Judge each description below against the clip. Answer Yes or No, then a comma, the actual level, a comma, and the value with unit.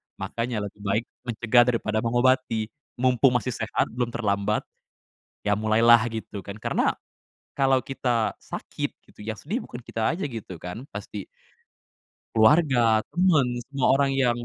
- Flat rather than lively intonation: No, average, 3.1 semitones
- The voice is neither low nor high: No, low, 115 Hz